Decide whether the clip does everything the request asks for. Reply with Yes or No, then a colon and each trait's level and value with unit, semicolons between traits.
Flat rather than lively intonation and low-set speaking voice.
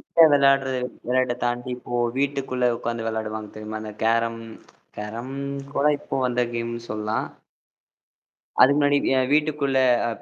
No: average, 3.3 semitones; low, 120 Hz